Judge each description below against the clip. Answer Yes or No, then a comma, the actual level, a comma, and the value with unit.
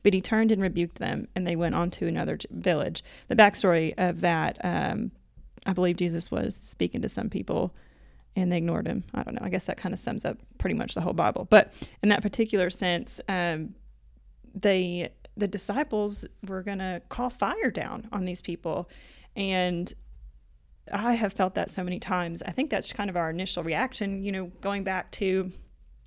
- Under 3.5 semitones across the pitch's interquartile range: Yes, average, 2.9 semitones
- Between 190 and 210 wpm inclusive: Yes, average, 195 wpm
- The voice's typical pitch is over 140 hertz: Yes, medium, 185 Hz